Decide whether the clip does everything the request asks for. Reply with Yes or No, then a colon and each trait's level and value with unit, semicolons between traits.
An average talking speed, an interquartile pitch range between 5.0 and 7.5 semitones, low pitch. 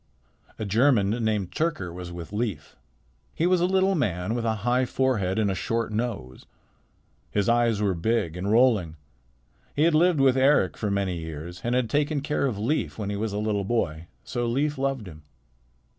Yes: average, 190 wpm; wide, 5.6 semitones; low, 110 Hz